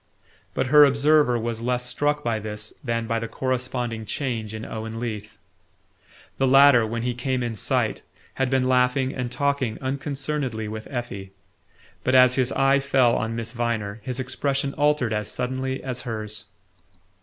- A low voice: Yes, low, 125 Hz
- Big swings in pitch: No, average, 2.9 semitones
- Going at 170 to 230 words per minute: No, average, 160 wpm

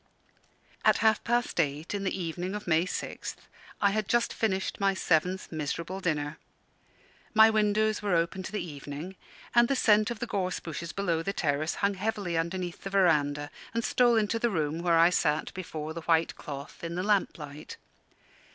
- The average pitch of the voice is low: No, medium, 180 Hz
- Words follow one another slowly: No, average, 180 wpm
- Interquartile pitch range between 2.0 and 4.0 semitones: No, average, 4.4 semitones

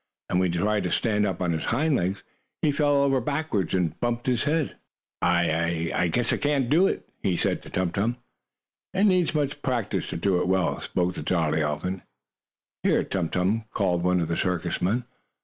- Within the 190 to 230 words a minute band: Yes, average, 200 wpm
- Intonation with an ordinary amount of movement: No, wide, 7.0 semitones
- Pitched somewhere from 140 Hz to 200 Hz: No, very low, 95 Hz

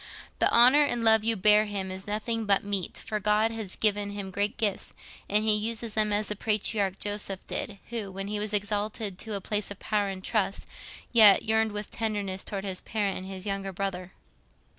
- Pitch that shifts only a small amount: Yes, narrow, 1.7 semitones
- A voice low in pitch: No, high, 205 Hz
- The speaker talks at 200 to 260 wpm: Yes, fast, 205 wpm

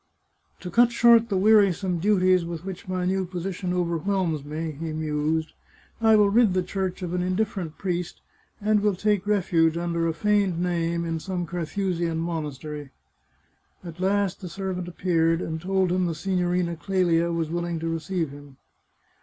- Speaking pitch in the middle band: Yes, medium, 180 Hz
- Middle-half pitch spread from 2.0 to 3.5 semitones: Yes, narrow, 2.6 semitones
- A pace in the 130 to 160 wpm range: No, average, 170 wpm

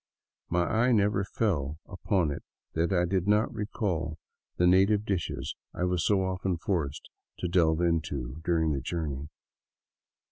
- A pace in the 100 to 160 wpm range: Yes, average, 145 wpm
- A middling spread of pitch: Yes, average, 3.6 semitones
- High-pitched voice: No, very low, 90 Hz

